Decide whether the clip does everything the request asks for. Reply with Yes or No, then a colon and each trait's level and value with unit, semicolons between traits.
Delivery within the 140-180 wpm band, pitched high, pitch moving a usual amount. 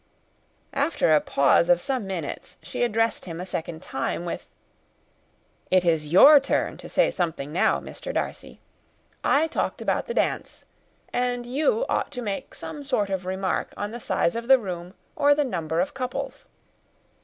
No: average, 165 wpm; high, 200 Hz; wide, 7.4 semitones